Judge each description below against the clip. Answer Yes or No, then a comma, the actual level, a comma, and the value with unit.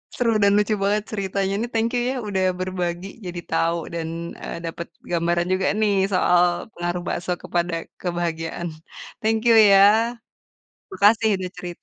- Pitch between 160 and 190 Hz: Yes, medium, 185 Hz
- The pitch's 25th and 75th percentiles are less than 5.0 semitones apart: Yes, average, 2.7 semitones